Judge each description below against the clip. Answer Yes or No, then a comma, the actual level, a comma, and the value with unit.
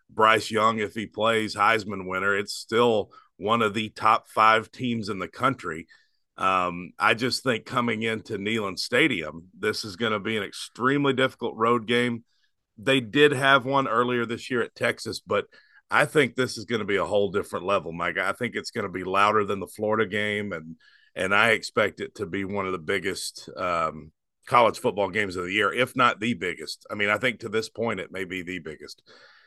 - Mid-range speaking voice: No, low, 110 Hz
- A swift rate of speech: Yes, fast, 210 wpm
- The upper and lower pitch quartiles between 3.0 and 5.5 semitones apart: Yes, average, 3.3 semitones